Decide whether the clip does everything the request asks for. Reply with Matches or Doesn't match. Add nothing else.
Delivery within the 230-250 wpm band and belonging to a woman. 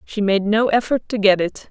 Matches